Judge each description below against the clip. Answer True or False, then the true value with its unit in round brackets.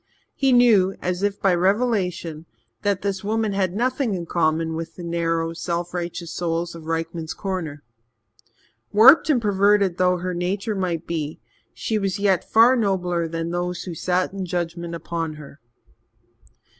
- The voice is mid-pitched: True (180 Hz)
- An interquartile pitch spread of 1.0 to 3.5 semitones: True (3.1 semitones)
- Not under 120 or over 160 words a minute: True (155 wpm)